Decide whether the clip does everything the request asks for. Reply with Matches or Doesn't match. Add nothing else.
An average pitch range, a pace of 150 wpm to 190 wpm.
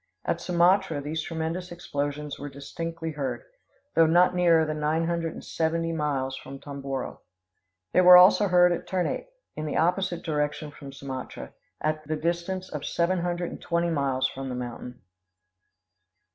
Matches